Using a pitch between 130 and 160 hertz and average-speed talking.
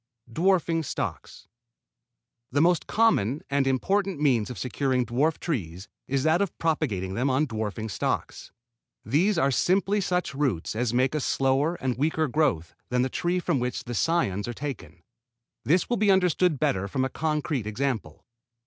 Yes: medium, 140 Hz; average, 155 wpm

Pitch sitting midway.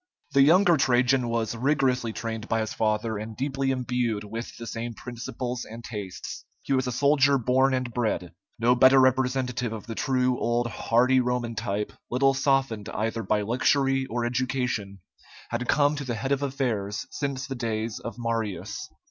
No: low, 125 Hz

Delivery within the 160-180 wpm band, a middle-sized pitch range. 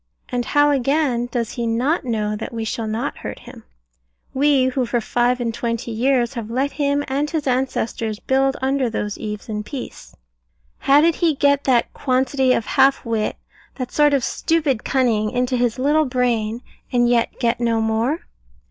Yes: average, 175 wpm; average, 3.1 semitones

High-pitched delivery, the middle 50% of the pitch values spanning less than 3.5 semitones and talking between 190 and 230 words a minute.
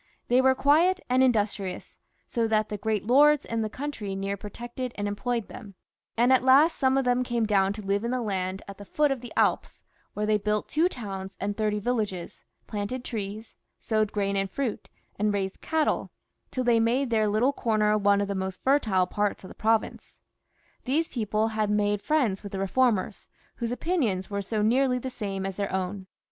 No: high, 215 Hz; average, 3.9 semitones; average, 200 wpm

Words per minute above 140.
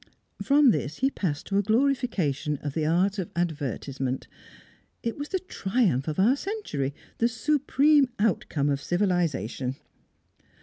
No: slow, 135 wpm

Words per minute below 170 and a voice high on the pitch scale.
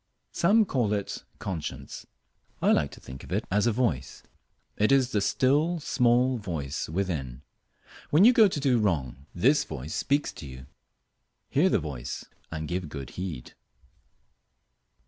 No: average, 150 wpm; low, 100 Hz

